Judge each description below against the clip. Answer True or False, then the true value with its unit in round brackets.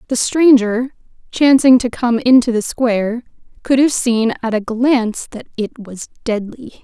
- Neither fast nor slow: True (160 wpm)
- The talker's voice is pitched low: False (240 Hz)